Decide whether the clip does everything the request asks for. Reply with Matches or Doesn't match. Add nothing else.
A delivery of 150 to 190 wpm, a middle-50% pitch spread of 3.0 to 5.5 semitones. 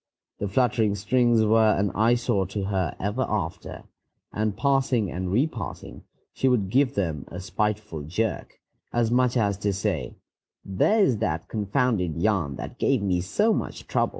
Matches